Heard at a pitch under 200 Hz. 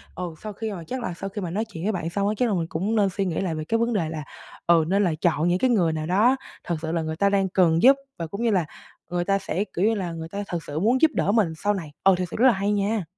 Yes: high, 190 Hz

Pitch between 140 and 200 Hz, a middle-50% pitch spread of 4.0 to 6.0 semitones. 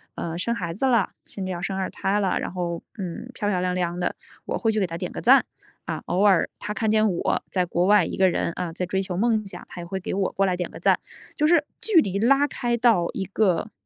No: high, 190 Hz; average, 3.4 semitones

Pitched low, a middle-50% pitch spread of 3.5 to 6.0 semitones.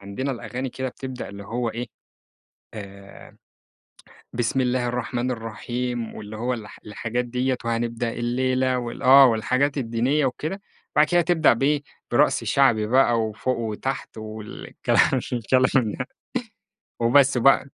No: low, 125 Hz; narrow, 2.4 semitones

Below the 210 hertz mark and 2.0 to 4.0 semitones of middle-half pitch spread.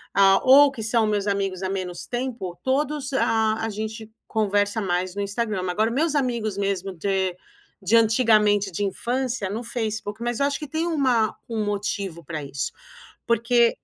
No: high, 215 Hz; average, 3.4 semitones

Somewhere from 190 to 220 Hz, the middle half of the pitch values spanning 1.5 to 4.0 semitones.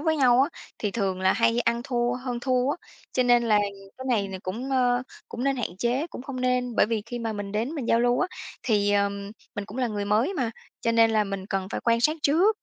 No: high, 235 Hz; average, 3.4 semitones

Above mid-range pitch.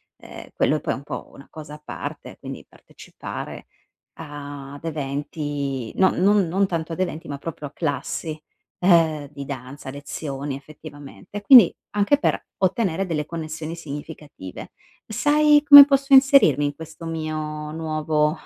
No: medium, 155 Hz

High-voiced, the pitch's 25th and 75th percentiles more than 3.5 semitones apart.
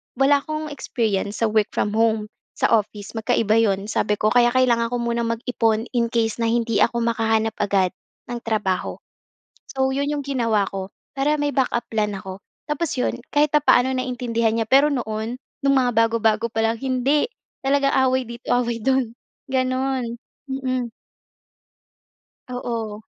No: high, 235 Hz; average, 2.9 semitones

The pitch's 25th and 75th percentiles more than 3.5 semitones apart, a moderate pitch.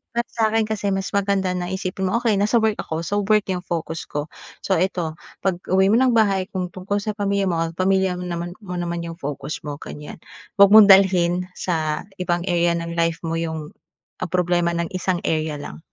No: average, 2.8 semitones; medium, 180 Hz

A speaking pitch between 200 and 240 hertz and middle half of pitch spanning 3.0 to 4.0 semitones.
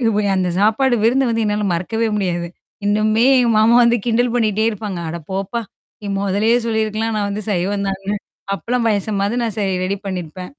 No: high, 210 Hz; narrow, 2.5 semitones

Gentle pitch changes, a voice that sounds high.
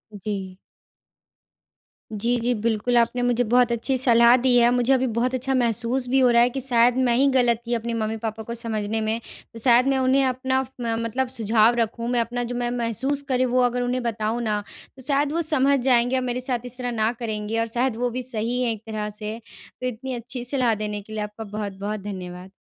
Yes: narrow, 2.3 semitones; high, 235 Hz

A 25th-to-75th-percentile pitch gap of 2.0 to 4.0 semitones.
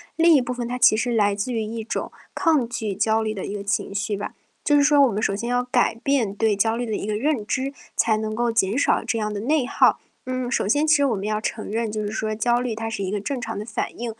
Yes: average, 2.8 semitones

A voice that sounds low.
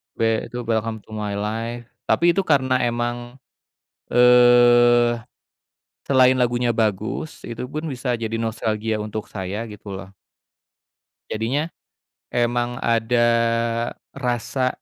Yes: low, 120 Hz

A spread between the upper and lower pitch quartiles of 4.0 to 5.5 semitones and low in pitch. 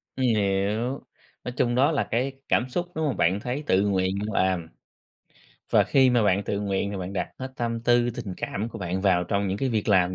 Yes: average, 4.4 semitones; low, 105 Hz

